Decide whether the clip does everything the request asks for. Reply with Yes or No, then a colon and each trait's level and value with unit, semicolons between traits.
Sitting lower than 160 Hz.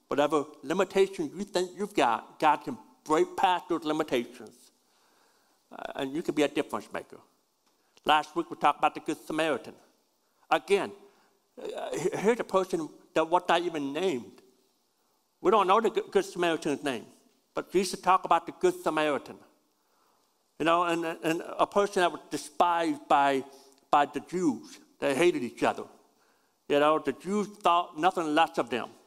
No: medium, 170 Hz